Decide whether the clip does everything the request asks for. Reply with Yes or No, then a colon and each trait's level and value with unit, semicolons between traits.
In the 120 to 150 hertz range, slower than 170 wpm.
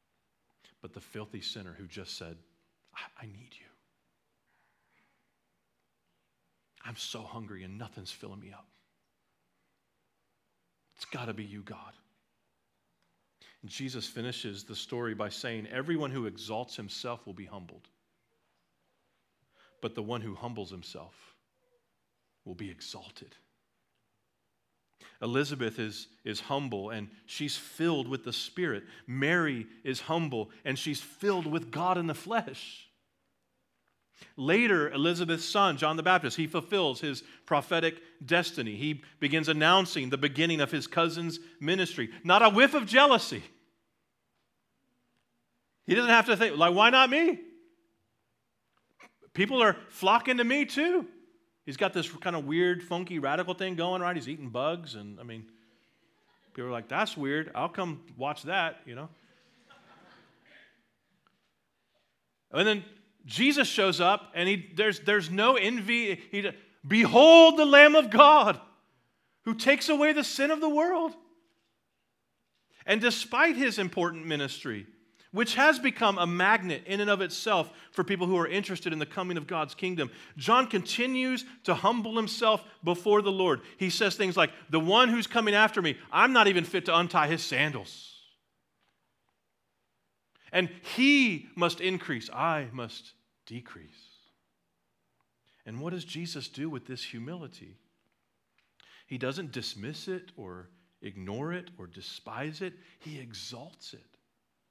No: medium, 165 Hz; average, 140 wpm